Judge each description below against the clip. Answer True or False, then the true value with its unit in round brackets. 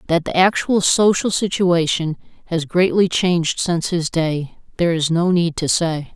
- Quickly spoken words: False (165 wpm)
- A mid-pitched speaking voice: True (170 Hz)